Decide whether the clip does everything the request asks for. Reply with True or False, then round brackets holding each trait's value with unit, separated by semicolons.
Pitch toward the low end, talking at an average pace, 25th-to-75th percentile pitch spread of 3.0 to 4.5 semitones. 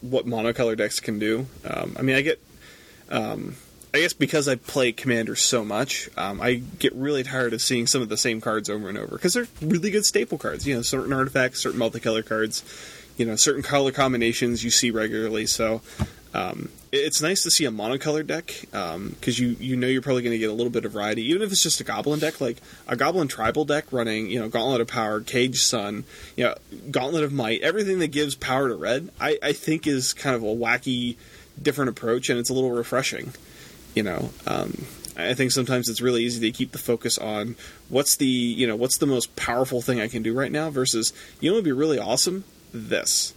False (125 Hz; 225 wpm; 3.4 semitones)